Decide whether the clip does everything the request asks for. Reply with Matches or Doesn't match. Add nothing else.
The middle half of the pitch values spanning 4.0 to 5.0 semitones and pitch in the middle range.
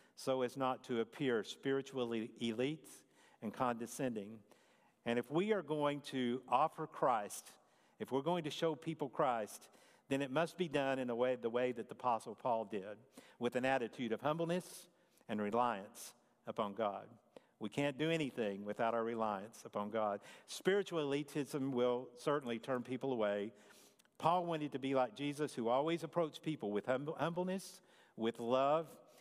Doesn't match